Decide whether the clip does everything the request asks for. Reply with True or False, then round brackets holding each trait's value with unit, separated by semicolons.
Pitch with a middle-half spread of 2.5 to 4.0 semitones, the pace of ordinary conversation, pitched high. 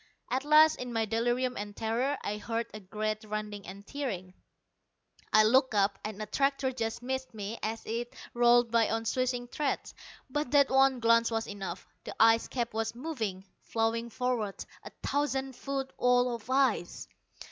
True (3.2 semitones; 170 wpm; 230 Hz)